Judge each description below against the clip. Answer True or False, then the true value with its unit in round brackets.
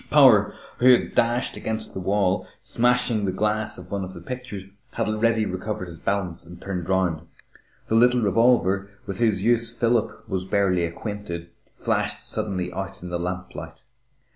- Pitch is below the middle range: True (100 Hz)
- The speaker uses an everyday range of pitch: True (3.7 semitones)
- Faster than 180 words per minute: False (165 wpm)